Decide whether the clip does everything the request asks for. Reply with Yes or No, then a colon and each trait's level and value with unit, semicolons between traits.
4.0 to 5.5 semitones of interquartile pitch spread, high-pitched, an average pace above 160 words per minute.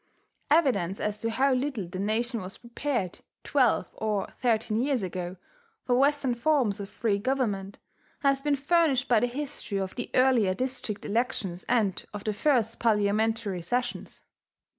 No: average, 4.6 semitones; high, 230 Hz; average, 150 wpm